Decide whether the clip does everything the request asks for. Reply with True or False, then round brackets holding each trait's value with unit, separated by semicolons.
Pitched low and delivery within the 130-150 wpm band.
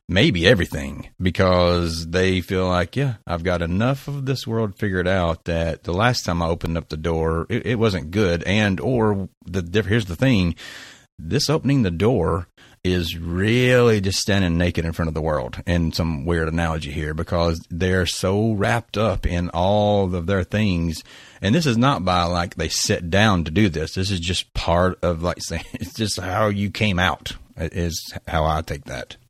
False (90 Hz; 190 wpm)